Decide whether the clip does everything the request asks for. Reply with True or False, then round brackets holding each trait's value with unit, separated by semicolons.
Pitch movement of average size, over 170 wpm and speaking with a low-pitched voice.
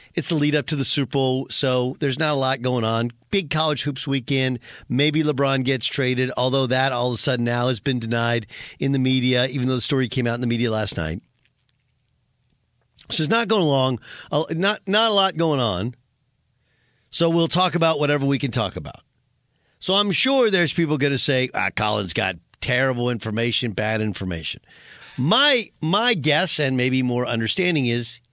True (3.8 semitones; 190 wpm; 130 Hz)